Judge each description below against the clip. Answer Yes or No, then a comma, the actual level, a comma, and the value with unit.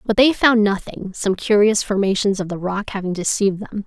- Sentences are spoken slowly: No, average, 200 wpm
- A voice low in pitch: No, high, 205 Hz